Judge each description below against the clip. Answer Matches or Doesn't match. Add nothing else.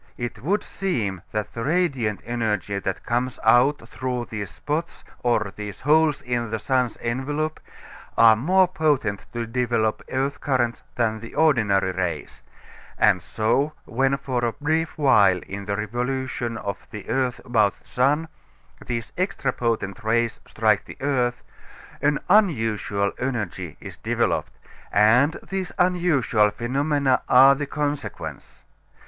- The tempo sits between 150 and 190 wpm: Doesn't match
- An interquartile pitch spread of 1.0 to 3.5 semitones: Doesn't match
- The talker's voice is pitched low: Matches